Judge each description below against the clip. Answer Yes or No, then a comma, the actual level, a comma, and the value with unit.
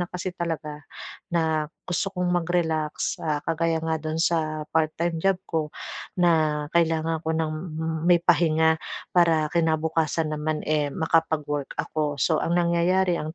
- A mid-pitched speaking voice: Yes, medium, 160 Hz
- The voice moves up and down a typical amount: No, narrow, 1.7 semitones